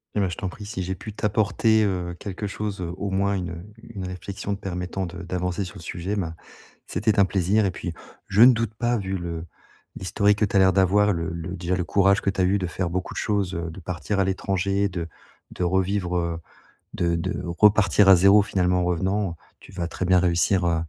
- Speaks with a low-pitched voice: Yes, very low, 95 Hz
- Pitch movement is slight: Yes, narrow, 2.3 semitones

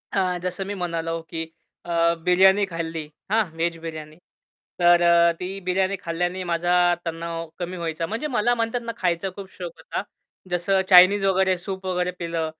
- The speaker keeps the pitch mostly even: Yes, narrow, 2.3 semitones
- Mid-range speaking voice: Yes, medium, 180 Hz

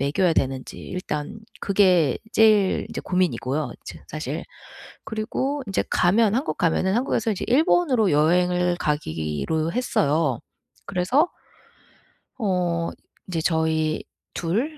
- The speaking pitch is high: No, medium, 180 Hz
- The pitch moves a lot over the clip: Yes, wide, 5.7 semitones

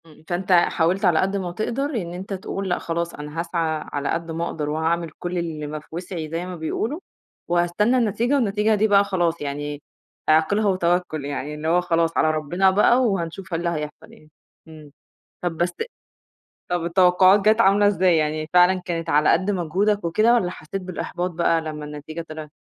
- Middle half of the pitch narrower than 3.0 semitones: No, average, 3.4 semitones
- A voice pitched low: No, medium, 175 Hz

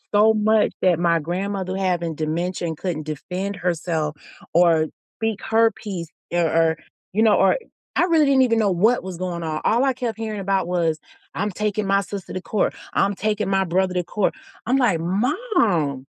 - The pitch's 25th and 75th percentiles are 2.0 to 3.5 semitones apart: No, average, 4.1 semitones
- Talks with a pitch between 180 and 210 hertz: Yes, high, 190 Hz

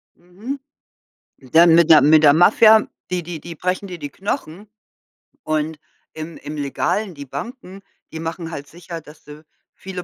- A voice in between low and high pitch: Yes, medium, 165 Hz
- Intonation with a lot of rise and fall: No, average, 3.0 semitones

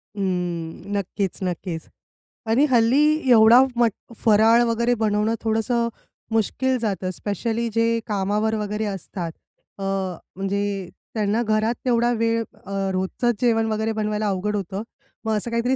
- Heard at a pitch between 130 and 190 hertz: No, high, 220 Hz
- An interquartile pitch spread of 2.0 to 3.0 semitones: Yes, narrow, 2.6 semitones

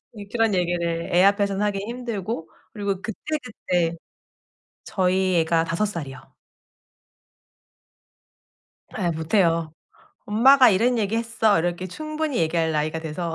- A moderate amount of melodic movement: Yes, average, 4.8 semitones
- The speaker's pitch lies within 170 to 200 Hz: Yes, high, 190 Hz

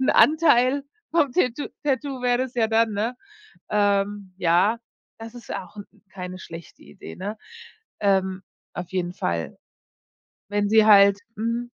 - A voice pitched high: Yes, high, 210 Hz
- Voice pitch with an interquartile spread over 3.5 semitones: Yes, average, 4.2 semitones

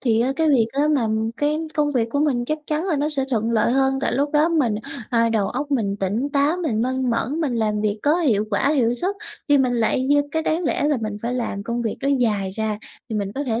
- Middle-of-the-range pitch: No, very high, 255 Hz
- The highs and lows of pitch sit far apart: No, average, 4.7 semitones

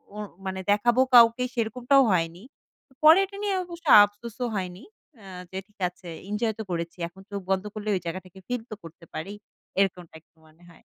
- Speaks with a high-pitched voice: Yes, high, 205 Hz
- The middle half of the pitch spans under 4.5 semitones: No, average, 5.0 semitones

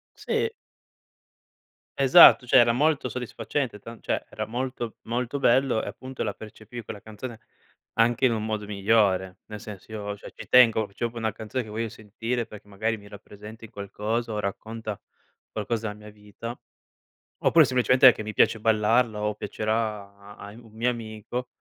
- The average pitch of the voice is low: Yes, low, 110 Hz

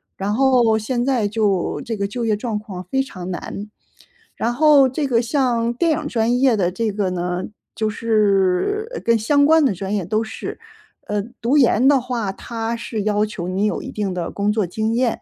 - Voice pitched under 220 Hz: No, high, 225 Hz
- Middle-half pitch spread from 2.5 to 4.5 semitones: Yes, average, 3.8 semitones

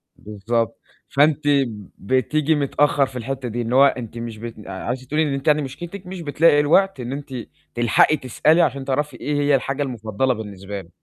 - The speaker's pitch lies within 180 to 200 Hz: No, low, 135 Hz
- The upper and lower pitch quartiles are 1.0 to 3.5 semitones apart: No, average, 3.9 semitones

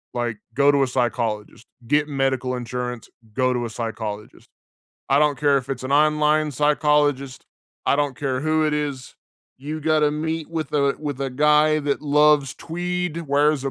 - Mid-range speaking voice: Yes, medium, 145 Hz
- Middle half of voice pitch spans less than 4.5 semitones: Yes, average, 2.8 semitones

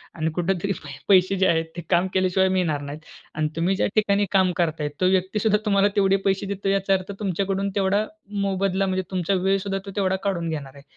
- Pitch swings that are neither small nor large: No, narrow, 2.0 semitones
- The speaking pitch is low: No, high, 190 Hz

